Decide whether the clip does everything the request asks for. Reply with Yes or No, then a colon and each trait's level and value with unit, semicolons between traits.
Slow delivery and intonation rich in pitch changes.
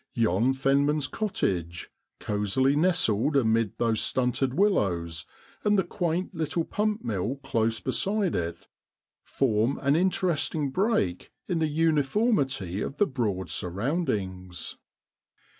Yes: slow, 115 wpm; wide, 8.0 semitones